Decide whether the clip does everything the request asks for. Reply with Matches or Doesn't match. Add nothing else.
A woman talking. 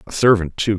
Doesn't match